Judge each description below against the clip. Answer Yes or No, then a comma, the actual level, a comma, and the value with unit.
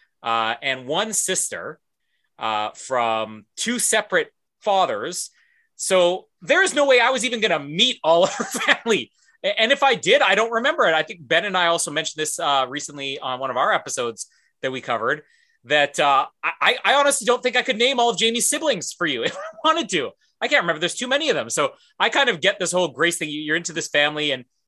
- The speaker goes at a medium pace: No, fast, 220 wpm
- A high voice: Yes, high, 195 Hz